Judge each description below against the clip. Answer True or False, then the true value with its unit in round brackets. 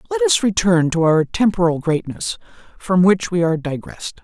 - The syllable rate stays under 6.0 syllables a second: True (5.3 syllables/s)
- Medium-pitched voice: True (175 Hz)